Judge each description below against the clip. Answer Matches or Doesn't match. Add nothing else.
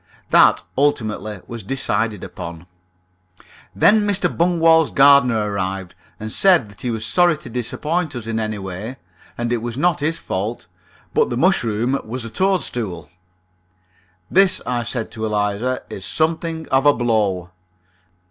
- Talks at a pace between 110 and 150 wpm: Matches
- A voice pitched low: Matches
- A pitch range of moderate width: Doesn't match